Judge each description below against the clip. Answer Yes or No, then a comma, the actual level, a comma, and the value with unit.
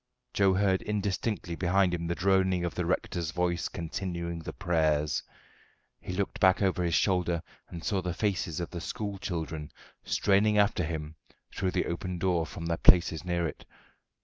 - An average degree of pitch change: No, narrow, 2.2 semitones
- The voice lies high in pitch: No, very low, 90 Hz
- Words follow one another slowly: No, average, 170 wpm